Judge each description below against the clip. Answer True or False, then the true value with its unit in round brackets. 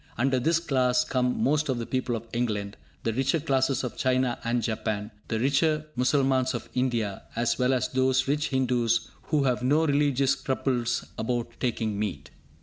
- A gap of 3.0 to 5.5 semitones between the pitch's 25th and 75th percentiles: False (2.5 semitones)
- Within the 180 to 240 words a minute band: False (170 wpm)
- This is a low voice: True (125 Hz)